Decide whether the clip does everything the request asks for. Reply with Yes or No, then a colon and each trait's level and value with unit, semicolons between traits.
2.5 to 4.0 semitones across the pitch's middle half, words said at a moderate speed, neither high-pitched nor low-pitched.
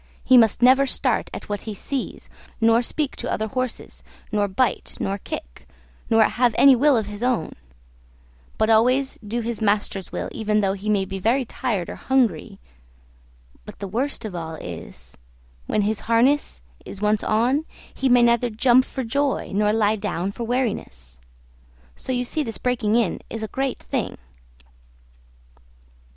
No: average, 3.6 semitones; average, 165 wpm; high, 225 Hz